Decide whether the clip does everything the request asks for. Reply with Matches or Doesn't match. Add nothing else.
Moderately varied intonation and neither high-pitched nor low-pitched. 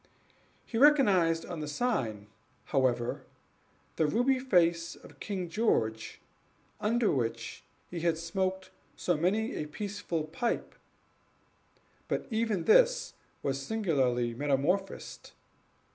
Doesn't match